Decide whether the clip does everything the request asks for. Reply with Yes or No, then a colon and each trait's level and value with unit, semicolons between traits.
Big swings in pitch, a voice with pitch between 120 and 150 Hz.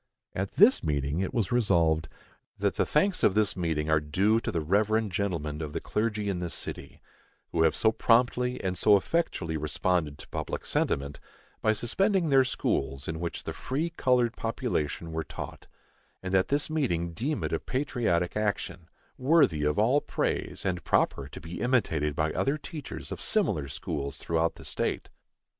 No: wide, 7.4 semitones; very low, 95 Hz